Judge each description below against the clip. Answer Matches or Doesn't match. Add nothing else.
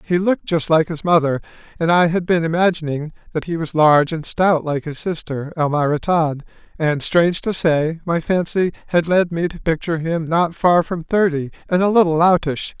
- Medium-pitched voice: Matches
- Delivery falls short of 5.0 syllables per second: Doesn't match